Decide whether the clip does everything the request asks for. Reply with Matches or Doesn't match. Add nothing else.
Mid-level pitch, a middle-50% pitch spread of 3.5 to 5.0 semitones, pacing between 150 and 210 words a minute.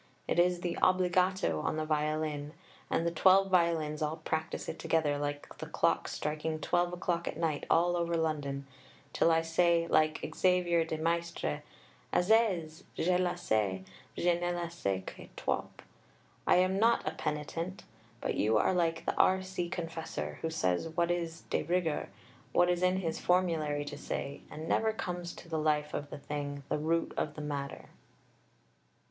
Doesn't match